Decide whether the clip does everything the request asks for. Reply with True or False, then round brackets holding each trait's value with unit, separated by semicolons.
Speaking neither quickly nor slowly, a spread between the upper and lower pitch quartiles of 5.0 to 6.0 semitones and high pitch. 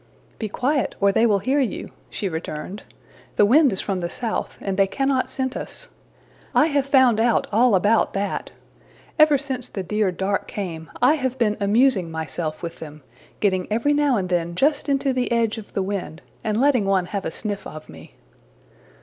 True (190 wpm; 5.6 semitones; 210 Hz)